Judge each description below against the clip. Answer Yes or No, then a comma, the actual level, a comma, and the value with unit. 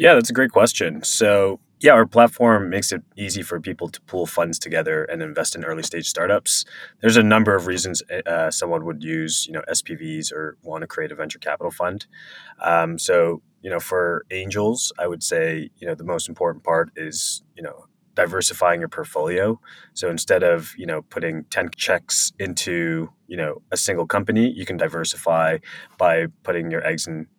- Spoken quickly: No, average, 190 wpm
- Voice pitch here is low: Yes, very low, 95 Hz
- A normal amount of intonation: No, wide, 5.8 semitones